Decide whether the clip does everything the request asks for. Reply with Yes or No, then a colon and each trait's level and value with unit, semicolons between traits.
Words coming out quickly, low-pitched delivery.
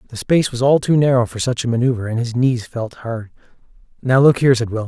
Yes: fast, 245 wpm; low, 125 Hz